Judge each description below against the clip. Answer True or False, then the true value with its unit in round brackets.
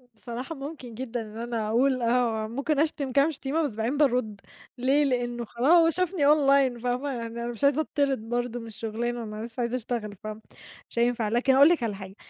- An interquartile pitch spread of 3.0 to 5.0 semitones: True (3.4 semitones)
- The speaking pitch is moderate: False (245 Hz)